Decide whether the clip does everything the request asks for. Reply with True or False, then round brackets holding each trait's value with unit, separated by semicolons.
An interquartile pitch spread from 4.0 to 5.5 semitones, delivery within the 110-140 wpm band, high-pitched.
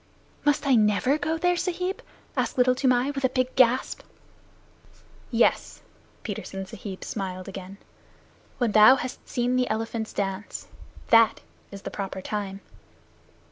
True (4.6 semitones; 135 wpm; 230 Hz)